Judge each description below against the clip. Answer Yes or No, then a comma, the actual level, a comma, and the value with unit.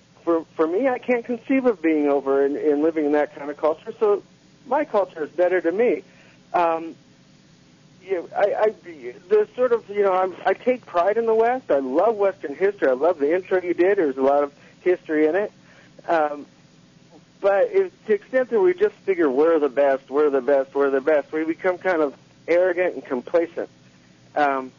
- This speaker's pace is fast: Yes, fast, 210 wpm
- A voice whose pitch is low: No, medium, 170 Hz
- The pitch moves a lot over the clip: Yes, wide, 7.6 semitones